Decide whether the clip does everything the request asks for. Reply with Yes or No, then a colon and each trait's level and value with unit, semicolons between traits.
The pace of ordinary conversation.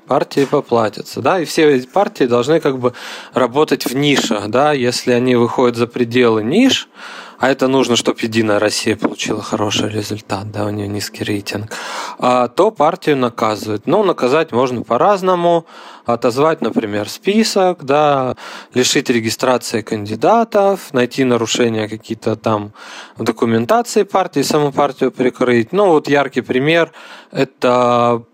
Yes: average, 135 wpm